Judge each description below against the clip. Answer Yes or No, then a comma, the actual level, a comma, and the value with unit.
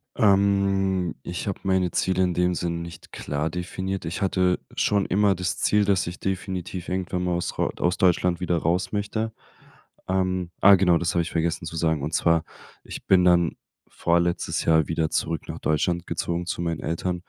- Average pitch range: No, narrow, 2.0 semitones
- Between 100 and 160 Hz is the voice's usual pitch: No, very low, 90 Hz